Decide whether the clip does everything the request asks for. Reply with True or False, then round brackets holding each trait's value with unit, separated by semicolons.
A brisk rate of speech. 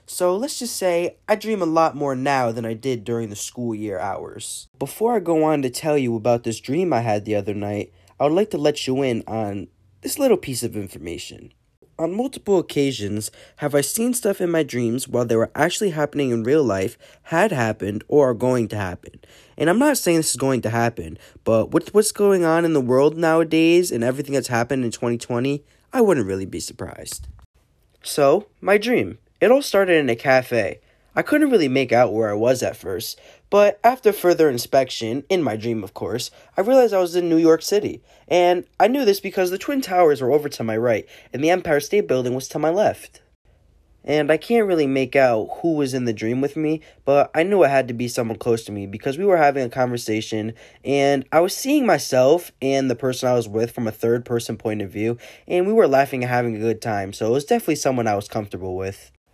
True (225 wpm)